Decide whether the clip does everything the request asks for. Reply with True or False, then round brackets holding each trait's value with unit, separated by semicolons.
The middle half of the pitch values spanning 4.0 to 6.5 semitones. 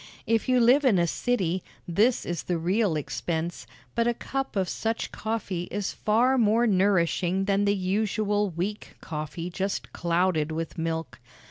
True (4.4 semitones)